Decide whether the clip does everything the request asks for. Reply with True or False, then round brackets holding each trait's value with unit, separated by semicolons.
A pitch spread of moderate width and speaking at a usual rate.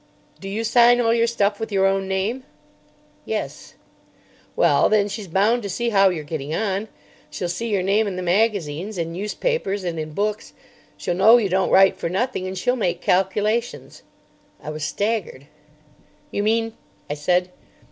True (3.6 semitones; 170 wpm)